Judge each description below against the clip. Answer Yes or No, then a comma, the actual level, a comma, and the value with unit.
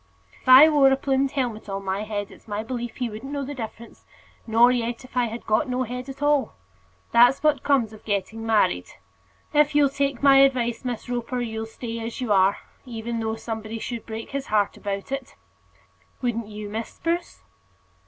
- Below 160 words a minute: No, average, 195 wpm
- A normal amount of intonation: Yes, average, 3.4 semitones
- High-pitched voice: Yes, high, 235 Hz